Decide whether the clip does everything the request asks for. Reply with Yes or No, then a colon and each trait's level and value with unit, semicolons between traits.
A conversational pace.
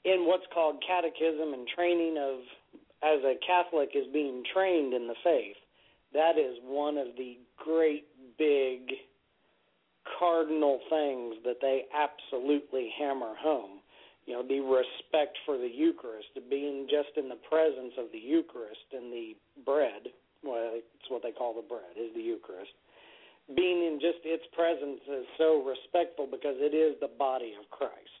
Yes: average, 155 wpm